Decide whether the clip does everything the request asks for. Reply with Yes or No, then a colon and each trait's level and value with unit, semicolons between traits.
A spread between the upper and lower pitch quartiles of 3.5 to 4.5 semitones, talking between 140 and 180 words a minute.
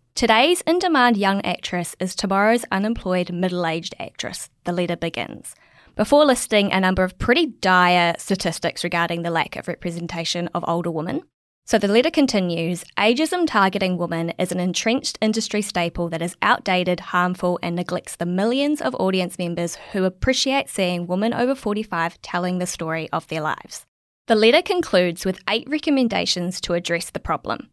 Yes: average, 4.1 semitones; average, 160 wpm